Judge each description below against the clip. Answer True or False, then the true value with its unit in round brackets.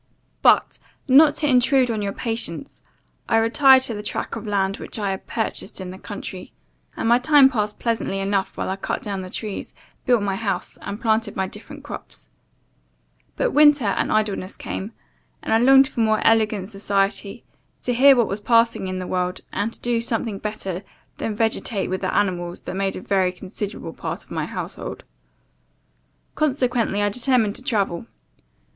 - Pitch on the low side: False (215 Hz)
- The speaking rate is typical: True (175 wpm)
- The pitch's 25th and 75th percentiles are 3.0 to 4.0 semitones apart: True (3.6 semitones)